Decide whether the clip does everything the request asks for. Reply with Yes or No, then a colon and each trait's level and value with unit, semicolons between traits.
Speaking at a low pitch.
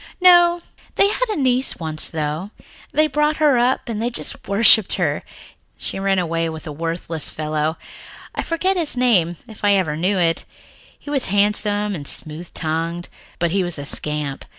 No: high, 195 Hz